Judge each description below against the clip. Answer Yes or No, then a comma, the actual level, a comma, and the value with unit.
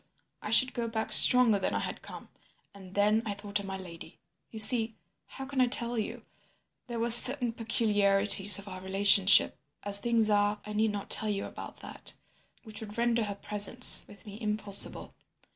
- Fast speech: No, average, 175 wpm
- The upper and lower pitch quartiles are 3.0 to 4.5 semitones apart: No, narrow, 2.5 semitones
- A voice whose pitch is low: No, high, 210 Hz